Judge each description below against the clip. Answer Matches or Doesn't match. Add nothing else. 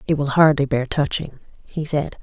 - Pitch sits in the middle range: Matches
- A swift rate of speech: Doesn't match